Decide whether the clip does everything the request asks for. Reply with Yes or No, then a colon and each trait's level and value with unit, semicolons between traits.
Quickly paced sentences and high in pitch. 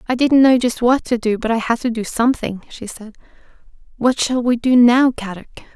Yes: fast, 220 wpm; high, 240 Hz